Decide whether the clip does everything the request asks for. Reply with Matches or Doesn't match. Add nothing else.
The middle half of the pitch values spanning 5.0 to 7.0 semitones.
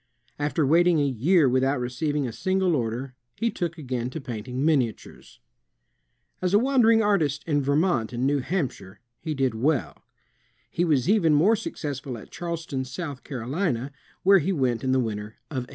Matches